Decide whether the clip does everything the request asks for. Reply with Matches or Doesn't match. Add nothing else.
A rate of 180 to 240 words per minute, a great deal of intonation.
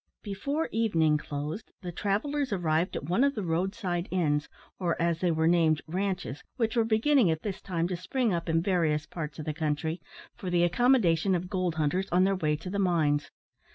Doesn't match